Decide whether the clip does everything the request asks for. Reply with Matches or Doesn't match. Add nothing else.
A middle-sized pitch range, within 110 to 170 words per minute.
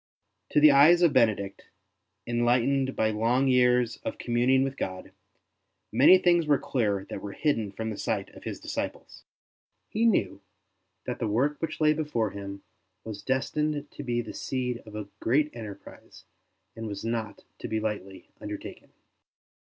Matches